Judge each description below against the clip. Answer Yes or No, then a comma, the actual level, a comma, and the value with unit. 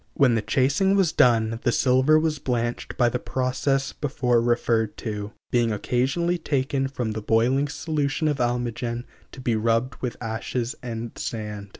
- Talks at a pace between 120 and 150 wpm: No, average, 160 wpm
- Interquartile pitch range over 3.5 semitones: No, average, 3.0 semitones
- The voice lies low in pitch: Yes, low, 125 Hz